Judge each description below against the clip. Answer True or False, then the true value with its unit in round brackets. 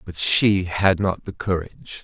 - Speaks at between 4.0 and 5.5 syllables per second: True (4.2 syllables/s)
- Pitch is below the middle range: True (95 Hz)